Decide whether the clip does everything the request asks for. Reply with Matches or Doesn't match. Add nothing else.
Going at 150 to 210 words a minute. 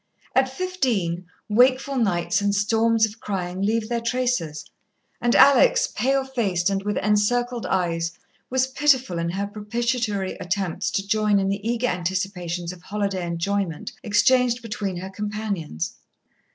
Doesn't match